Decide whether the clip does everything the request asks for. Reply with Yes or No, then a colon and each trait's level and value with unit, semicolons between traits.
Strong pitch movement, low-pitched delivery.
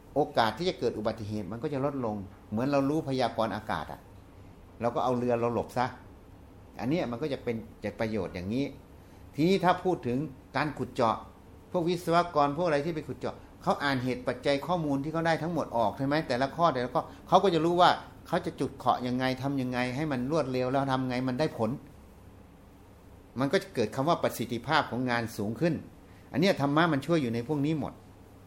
Yes: wide, 6.3 semitones; low, 125 Hz